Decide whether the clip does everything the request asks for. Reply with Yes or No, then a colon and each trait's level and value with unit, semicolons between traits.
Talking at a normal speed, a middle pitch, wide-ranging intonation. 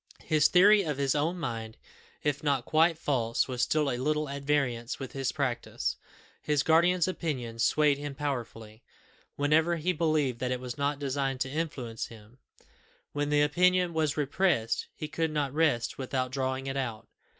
No: average, 170 wpm; medium, 145 Hz; average, 3.4 semitones